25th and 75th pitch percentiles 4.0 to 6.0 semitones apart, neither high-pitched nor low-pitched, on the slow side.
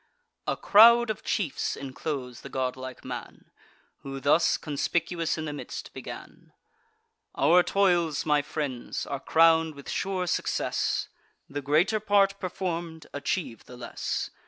Yes: average, 4.5 semitones; medium, 160 Hz; slow, 130 wpm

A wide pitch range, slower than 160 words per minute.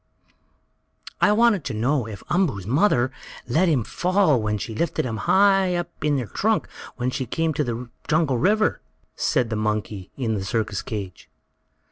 No: wide, 7.8 semitones; average, 165 wpm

